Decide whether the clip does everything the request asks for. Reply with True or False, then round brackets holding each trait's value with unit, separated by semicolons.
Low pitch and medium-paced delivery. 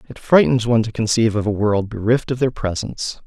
False (110 Hz; 220 wpm)